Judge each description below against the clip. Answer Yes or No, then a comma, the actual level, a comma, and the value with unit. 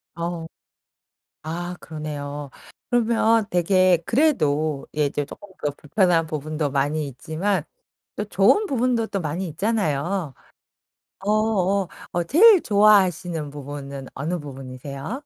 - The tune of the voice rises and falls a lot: Yes, wide, 5.8 semitones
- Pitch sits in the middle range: Yes, medium, 170 Hz